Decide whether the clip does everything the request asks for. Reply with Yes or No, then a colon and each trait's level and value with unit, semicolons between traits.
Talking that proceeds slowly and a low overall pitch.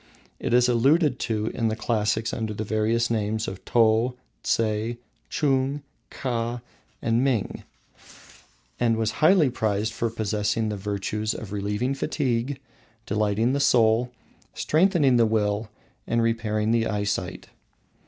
Yes: slow, 130 wpm; low, 115 Hz